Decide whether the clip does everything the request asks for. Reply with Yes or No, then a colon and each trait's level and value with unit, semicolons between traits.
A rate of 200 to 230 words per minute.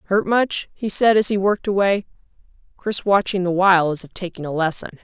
Yes: fast, 205 wpm